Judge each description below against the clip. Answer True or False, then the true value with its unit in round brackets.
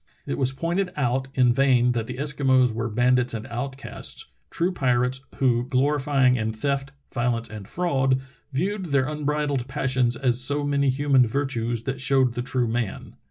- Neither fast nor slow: True (170 wpm)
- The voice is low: True (130 Hz)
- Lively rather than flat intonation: False (2.5 semitones)